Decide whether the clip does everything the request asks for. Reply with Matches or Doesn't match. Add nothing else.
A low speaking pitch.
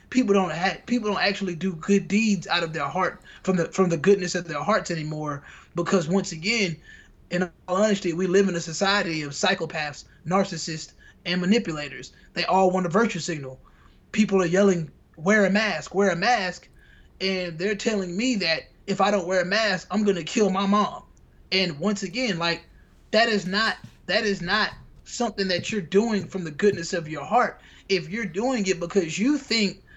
Doesn't match